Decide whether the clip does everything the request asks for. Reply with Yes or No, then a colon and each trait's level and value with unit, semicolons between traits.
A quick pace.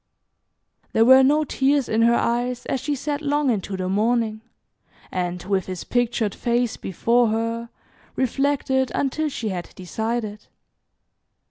No: slow, 135 wpm